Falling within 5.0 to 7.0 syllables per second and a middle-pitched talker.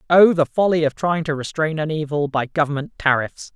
Yes: 5.5 syllables/s; medium, 155 Hz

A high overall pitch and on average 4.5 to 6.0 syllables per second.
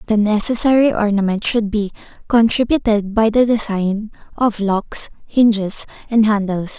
Yes: high, 215 Hz; 4.9 syllables/s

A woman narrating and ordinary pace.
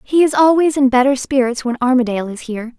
No: female; fast, 215 wpm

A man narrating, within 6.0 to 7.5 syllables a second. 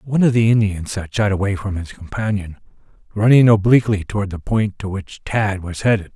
No: male; 5.6 syllables/s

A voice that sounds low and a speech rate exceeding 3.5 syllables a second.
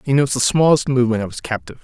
Yes: low, 125 Hz; 8.1 syllables/s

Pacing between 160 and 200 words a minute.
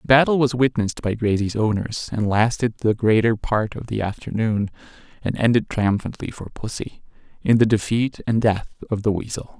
Yes: average, 175 wpm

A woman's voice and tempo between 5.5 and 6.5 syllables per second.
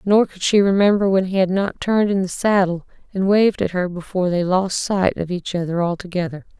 Yes: female; 5.7 syllables/s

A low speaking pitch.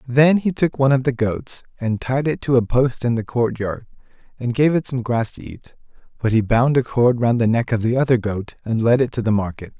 Yes: low, 120 Hz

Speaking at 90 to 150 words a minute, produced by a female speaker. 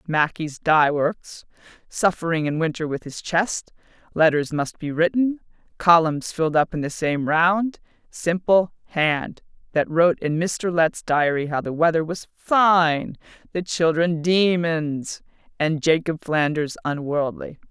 Yes: slow, 135 wpm; female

